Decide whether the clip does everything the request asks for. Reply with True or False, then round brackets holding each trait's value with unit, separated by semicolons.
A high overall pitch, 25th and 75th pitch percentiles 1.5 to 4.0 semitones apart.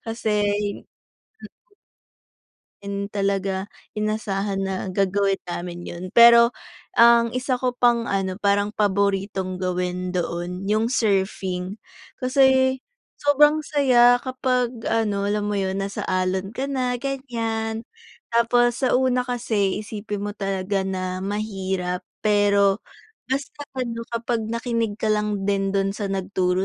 True (205 Hz; 3.5 semitones)